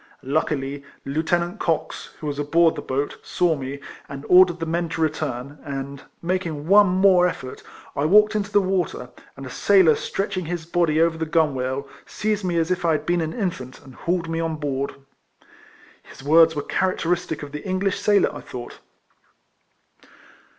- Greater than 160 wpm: Yes, average, 175 wpm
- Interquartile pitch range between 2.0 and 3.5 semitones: No, average, 3.9 semitones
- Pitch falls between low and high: Yes, medium, 165 Hz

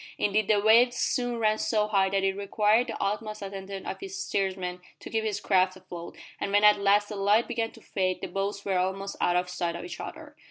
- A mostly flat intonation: Yes, narrow, 2.0 semitones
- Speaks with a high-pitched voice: Yes, high, 200 Hz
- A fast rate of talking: Yes, fast, 230 wpm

